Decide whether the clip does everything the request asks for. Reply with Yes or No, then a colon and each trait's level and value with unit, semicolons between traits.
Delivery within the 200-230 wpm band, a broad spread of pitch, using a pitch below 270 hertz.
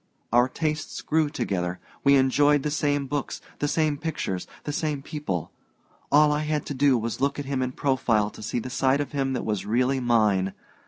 No: fast, 205 wpm; average, 3.6 semitones; low, 135 Hz